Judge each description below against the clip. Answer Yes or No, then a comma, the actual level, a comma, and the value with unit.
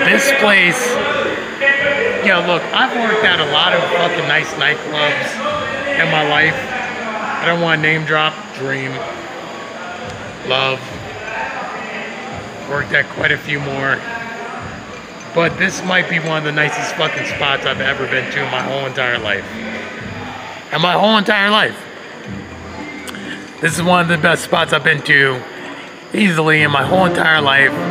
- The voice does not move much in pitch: No, average, 4.3 semitones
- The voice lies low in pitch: No, medium, 160 Hz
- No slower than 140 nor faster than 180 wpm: Yes, average, 150 wpm